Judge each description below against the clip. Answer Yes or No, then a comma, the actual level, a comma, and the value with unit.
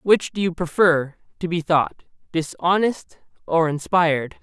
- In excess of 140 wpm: No, slow, 135 wpm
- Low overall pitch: No, medium, 170 Hz